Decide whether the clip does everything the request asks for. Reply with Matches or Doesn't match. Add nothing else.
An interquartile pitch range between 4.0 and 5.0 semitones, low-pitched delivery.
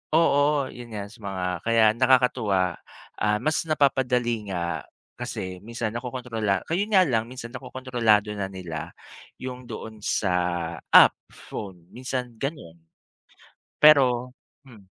Matches